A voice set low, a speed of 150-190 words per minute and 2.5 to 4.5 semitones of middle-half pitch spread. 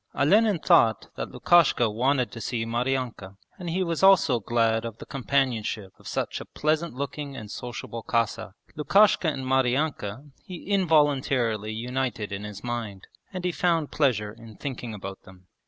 No: low, 125 Hz; average, 155 wpm; average, 5.3 semitones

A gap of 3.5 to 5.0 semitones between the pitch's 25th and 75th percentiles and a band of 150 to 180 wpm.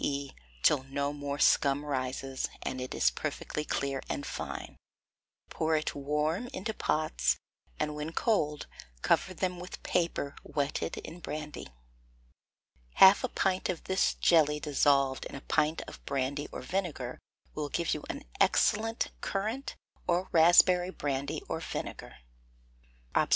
No: average, 4.1 semitones; average, 140 wpm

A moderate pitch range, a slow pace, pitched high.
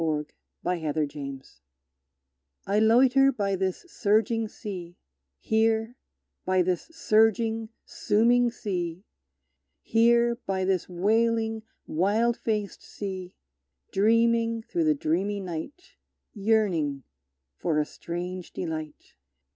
Yes: average, 4.4 semitones; slow, 100 wpm; high, 205 Hz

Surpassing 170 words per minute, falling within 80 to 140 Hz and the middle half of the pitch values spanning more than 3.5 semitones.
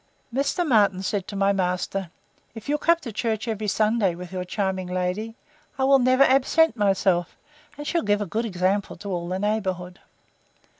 No: average, 180 wpm; high, 205 Hz; average, 4.0 semitones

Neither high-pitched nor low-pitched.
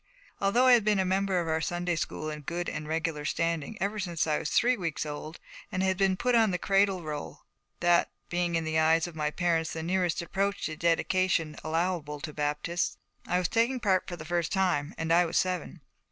Yes: medium, 175 Hz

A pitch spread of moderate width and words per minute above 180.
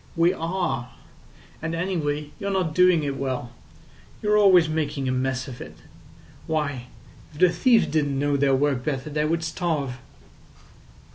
No: average, 3.9 semitones; average, 150 wpm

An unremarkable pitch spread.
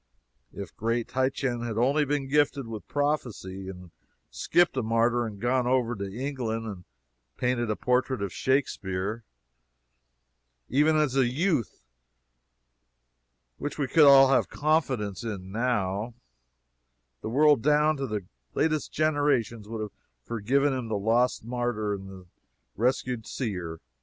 Yes: average, 4.3 semitones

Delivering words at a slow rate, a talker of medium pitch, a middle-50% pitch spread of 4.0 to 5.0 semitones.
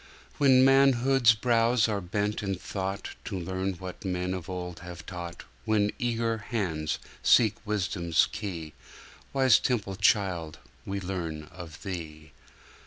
No: slow, 120 wpm; very low, 95 Hz; average, 4.3 semitones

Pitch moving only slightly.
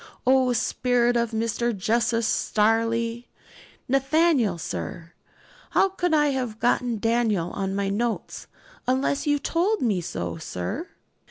No: average, 3.4 semitones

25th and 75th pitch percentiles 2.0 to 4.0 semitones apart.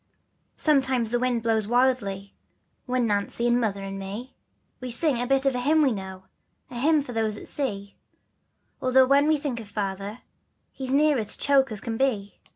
No: average, 4.4 semitones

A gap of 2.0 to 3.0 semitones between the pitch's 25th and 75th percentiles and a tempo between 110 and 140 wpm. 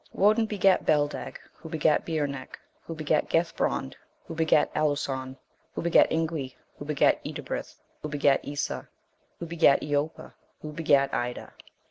Yes: narrow, 2.4 semitones; slow, 135 wpm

